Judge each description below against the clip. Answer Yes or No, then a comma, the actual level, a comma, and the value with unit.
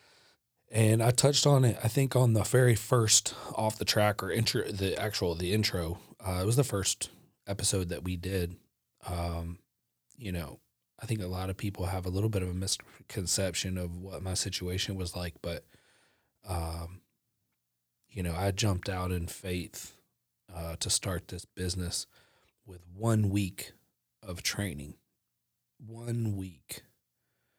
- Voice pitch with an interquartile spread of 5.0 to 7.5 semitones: No, average, 3.4 semitones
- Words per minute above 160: No, average, 155 wpm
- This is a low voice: Yes, very low, 95 Hz